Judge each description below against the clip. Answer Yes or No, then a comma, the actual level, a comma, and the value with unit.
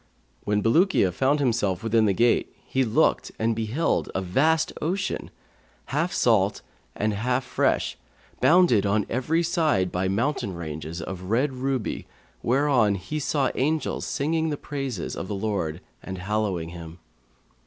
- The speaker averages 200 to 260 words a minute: No, average, 145 wpm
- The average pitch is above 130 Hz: No, low, 115 Hz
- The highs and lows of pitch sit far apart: Yes, wide, 7.0 semitones